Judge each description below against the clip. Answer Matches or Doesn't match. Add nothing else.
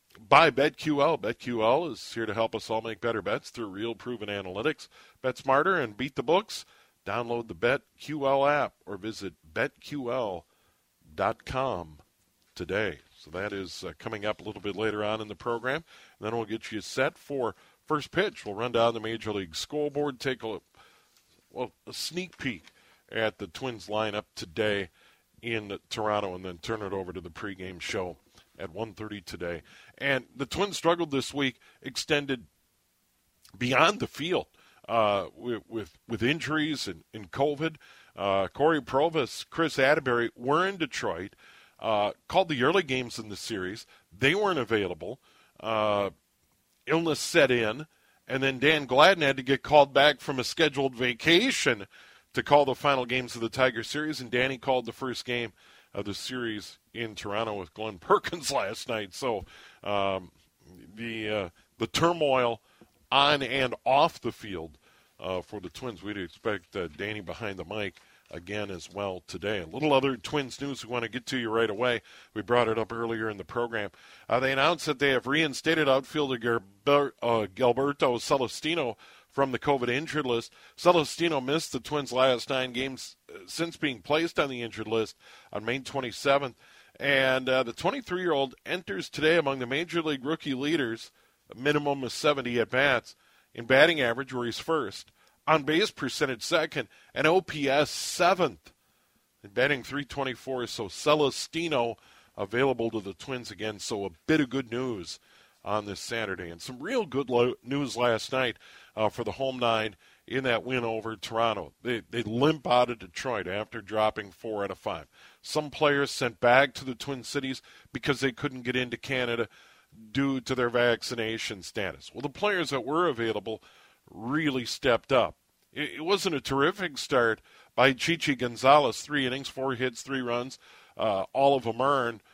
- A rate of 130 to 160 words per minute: Doesn't match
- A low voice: Matches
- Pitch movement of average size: Matches